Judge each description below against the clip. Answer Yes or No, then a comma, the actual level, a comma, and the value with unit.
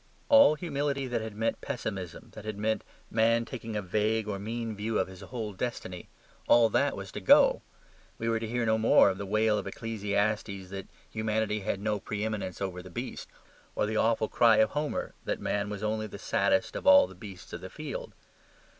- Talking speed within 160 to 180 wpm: No, average, 200 wpm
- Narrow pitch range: Yes, narrow, 2.0 semitones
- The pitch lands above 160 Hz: No, low, 110 Hz